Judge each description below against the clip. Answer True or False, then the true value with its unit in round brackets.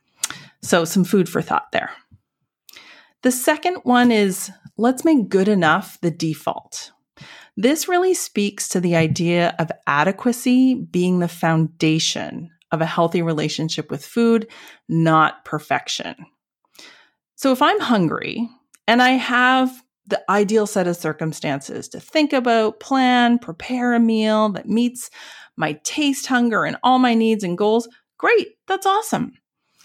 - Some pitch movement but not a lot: False (6.6 semitones)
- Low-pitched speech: False (220 Hz)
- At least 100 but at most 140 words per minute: True (135 wpm)